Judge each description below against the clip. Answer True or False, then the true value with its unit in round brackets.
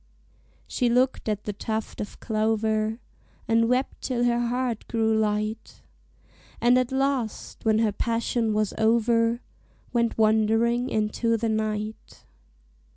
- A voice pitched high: True (225 Hz)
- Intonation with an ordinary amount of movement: False (1.7 semitones)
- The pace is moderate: False (125 wpm)